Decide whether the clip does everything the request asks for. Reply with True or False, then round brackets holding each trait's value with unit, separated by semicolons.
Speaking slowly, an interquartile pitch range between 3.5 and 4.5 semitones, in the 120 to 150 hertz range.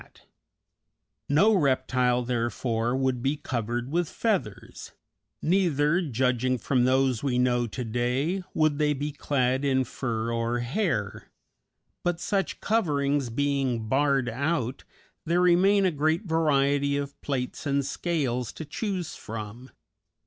True (125 wpm; 3.9 semitones; 135 Hz)